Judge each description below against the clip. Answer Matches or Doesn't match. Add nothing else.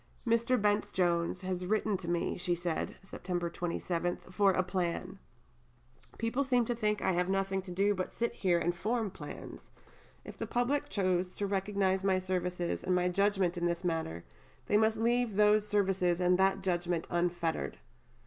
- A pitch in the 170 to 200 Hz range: Matches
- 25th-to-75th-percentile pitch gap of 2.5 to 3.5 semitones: Matches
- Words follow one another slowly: Doesn't match